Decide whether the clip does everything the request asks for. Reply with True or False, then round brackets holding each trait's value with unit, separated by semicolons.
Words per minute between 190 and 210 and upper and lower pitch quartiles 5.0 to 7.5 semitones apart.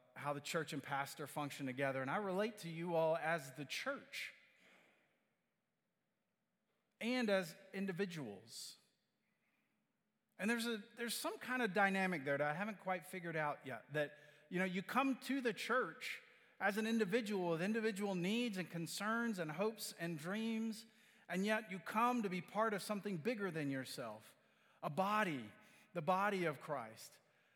False (160 wpm; 5.3 semitones)